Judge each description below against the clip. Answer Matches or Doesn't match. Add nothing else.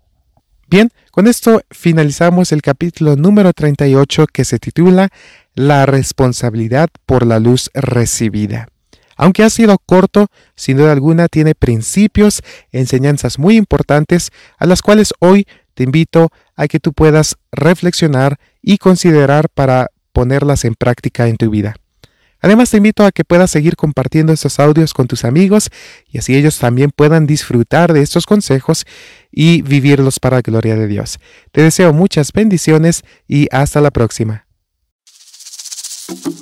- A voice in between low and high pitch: Matches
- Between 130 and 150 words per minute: Matches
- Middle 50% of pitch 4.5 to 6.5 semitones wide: Matches